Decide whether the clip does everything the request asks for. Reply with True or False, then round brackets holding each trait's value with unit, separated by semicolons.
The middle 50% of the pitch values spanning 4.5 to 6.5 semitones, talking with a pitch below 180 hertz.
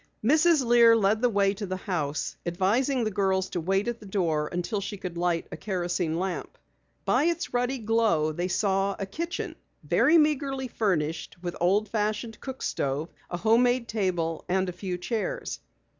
False (4.8 semitones; 200 Hz)